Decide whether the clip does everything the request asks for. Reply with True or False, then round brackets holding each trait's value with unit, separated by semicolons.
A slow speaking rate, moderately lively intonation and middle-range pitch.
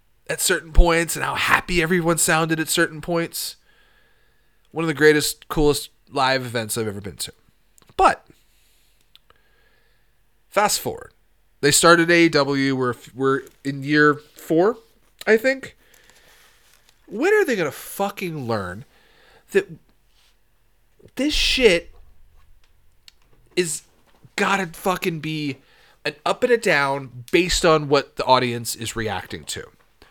False (120 wpm; 6.2 semitones; 155 Hz)